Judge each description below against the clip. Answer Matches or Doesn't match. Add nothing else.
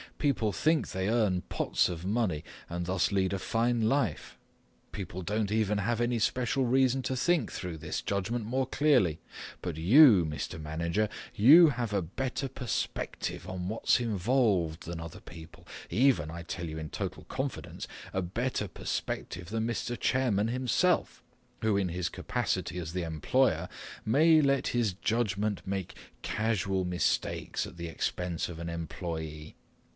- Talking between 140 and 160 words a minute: Matches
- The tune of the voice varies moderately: Doesn't match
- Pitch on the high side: Doesn't match